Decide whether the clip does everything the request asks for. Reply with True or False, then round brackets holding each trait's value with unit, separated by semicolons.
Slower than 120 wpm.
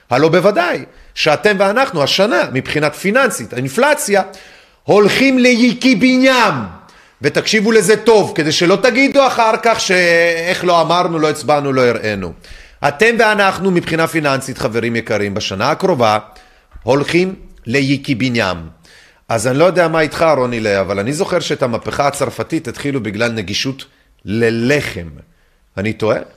False (125 wpm)